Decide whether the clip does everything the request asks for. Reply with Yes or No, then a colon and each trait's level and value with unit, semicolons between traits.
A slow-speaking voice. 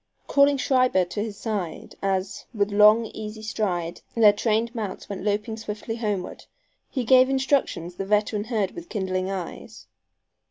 No: average, 150 wpm